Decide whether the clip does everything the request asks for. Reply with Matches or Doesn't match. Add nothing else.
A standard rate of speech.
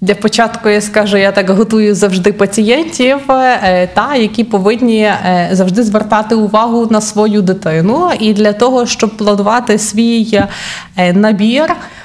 Matches